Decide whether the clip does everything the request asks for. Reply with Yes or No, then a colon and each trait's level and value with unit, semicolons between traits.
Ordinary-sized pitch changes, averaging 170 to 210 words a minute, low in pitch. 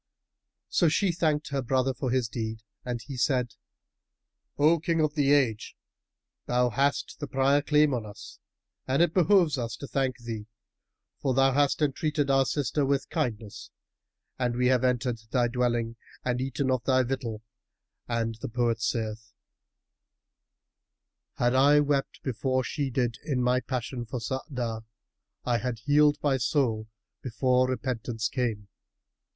No: average, 3.1 semitones; average, 150 wpm; low, 130 Hz